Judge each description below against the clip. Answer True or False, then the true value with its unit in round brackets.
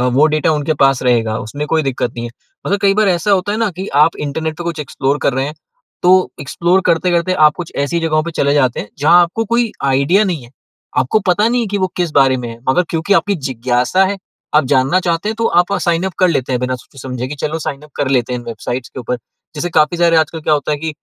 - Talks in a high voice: False (155 Hz)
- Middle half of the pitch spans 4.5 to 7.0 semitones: True (5.0 semitones)